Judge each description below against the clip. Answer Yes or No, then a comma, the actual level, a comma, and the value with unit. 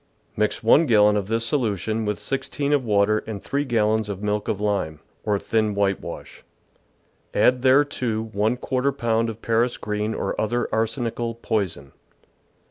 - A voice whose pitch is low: Yes, low, 110 Hz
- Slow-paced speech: No, average, 150 wpm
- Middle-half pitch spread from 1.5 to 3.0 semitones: Yes, narrow, 2.5 semitones